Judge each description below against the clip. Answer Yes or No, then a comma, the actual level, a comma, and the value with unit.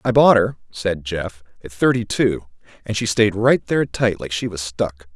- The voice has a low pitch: Yes, low, 100 Hz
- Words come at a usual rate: No, fast, 210 wpm